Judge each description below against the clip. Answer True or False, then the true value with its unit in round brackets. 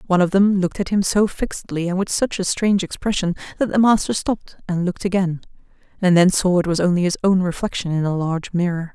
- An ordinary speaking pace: False (230 wpm)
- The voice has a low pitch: False (185 Hz)